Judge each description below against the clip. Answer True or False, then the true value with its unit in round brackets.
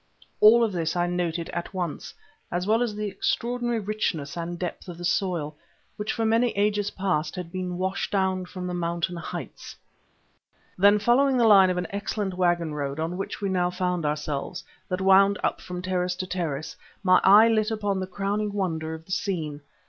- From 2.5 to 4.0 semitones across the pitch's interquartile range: True (2.9 semitones)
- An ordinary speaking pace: True (190 wpm)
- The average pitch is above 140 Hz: True (185 Hz)